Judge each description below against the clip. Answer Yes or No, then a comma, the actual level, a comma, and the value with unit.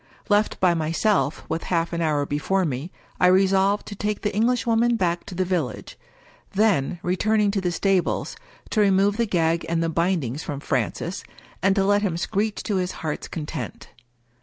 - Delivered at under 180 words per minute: No, average, 185 wpm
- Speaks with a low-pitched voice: No, medium, 185 Hz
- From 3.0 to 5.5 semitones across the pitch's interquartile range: Yes, average, 3.7 semitones